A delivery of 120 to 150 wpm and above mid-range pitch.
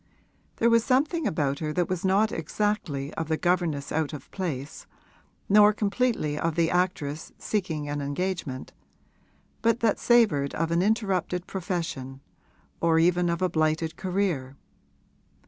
No: average, 140 wpm; medium, 170 Hz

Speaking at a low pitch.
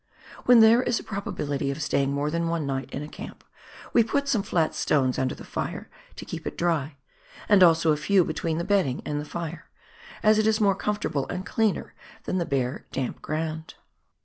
No: medium, 165 Hz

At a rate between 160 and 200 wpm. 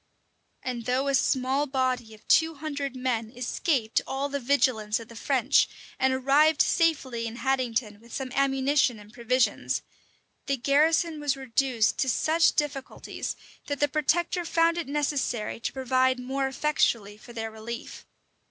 No: average, 150 wpm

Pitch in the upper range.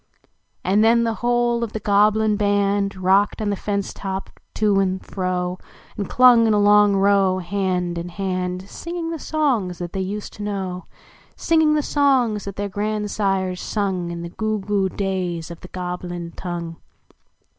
Yes: high, 200 Hz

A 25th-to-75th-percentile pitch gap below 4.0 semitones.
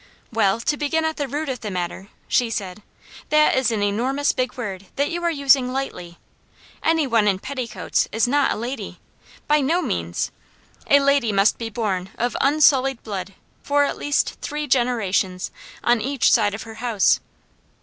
No: wide, 5.6 semitones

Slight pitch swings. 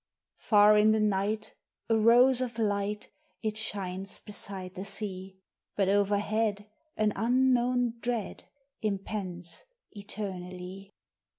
Yes: narrow, 2.2 semitones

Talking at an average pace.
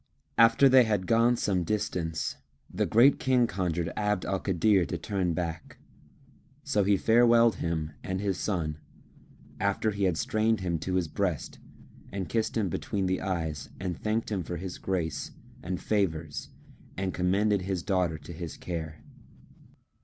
Yes: average, 155 wpm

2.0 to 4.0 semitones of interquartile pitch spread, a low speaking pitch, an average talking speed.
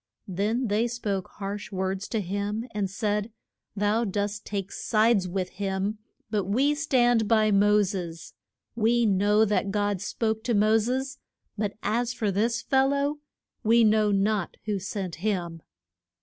No: narrow, 2.5 semitones; high, 210 Hz; average, 150 wpm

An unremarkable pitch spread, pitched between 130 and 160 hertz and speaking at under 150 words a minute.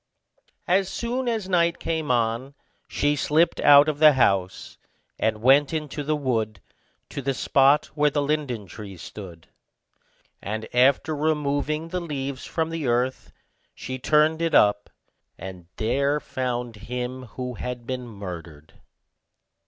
Yes: average, 4.9 semitones; low, 135 Hz; slow, 135 wpm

